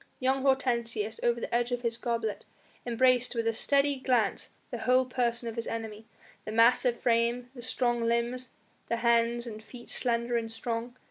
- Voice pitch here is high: Yes, high, 235 Hz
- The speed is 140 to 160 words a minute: No, average, 175 wpm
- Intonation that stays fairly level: Yes, narrow, 1.3 semitones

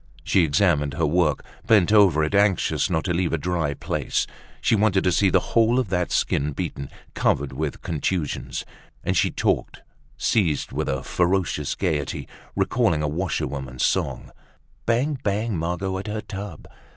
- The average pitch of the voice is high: No, very low, 90 Hz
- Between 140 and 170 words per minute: Yes, average, 160 wpm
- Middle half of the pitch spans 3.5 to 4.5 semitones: No, average, 5.0 semitones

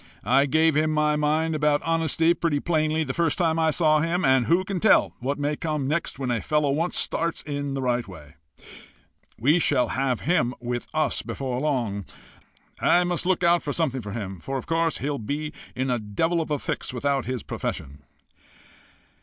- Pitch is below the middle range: No, medium, 150 Hz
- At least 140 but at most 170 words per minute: No, average, 195 wpm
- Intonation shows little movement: No, average, 4.0 semitones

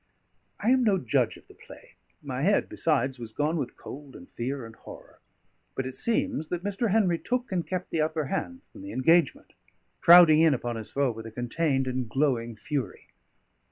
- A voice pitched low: No, medium, 150 Hz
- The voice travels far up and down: Yes, wide, 6.2 semitones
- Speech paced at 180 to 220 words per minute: Yes, average, 190 wpm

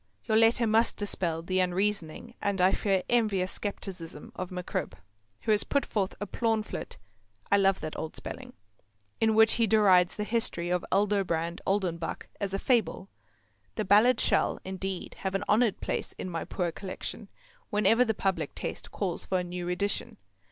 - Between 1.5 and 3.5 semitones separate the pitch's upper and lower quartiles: Yes, average, 3.0 semitones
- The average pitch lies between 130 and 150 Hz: No, high, 195 Hz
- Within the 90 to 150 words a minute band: No, average, 165 wpm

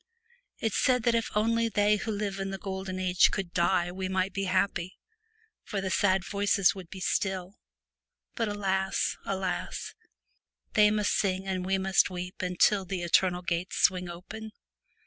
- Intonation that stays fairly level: Yes, narrow, 1.9 semitones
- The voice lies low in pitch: No, high, 190 Hz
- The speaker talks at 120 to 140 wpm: No, average, 175 wpm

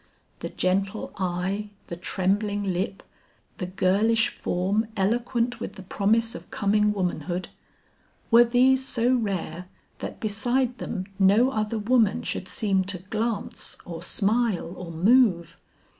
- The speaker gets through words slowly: Yes, slow, 130 wpm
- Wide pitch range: No, average, 3.7 semitones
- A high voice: Yes, high, 205 Hz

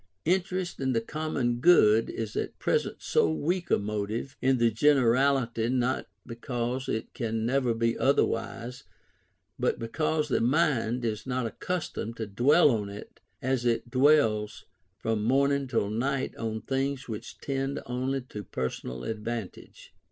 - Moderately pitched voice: No, low, 120 Hz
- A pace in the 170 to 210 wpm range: No, average, 145 wpm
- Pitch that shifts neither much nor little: Yes, average, 3.5 semitones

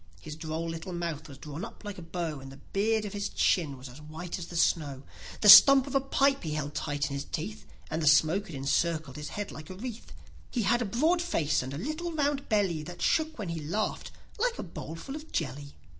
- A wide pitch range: Yes, wide, 6.4 semitones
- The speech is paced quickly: Yes, fast, 235 wpm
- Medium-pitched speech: Yes, medium, 170 Hz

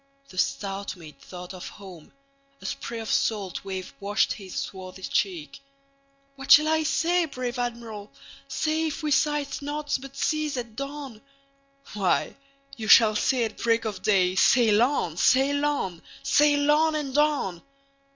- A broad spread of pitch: Yes, wide, 6.1 semitones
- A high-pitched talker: Yes, very high, 260 Hz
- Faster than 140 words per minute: No, slow, 135 wpm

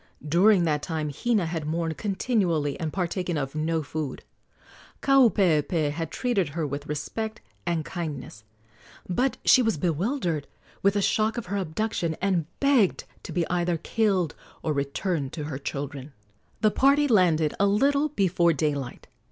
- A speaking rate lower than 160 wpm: Yes, average, 150 wpm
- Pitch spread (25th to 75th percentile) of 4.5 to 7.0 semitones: Yes, average, 5.2 semitones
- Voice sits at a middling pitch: Yes, medium, 170 Hz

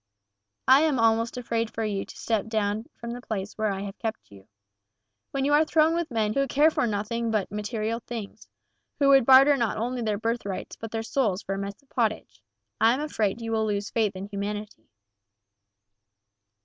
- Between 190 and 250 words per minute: Yes, average, 195 wpm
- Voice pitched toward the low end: No, high, 225 Hz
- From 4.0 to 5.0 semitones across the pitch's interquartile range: No, average, 3.1 semitones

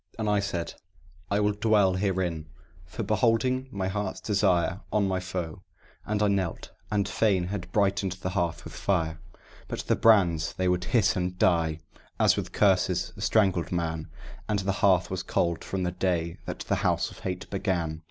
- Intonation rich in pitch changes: No, average, 2.8 semitones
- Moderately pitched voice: No, very low, 95 Hz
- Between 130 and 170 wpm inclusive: No, average, 180 wpm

